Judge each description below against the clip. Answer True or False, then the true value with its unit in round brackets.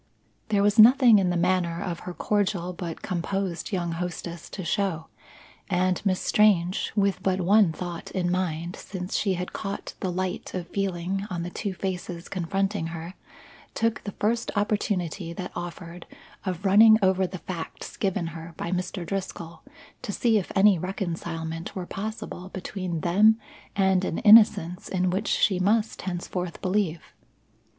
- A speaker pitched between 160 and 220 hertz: True (185 Hz)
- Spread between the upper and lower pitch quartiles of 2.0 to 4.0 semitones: True (2.5 semitones)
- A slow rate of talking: False (155 wpm)